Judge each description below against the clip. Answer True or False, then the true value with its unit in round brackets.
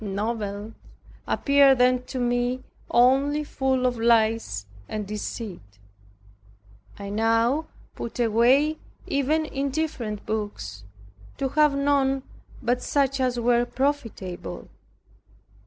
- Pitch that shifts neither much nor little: True (4.0 semitones)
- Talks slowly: True (100 wpm)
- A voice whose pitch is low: False (245 Hz)